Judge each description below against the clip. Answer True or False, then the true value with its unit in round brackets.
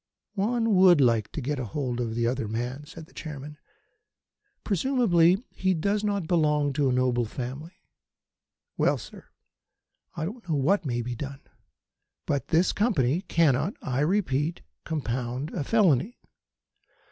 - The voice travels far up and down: True (6.3 semitones)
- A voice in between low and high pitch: True (150 Hz)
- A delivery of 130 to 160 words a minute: True (140 wpm)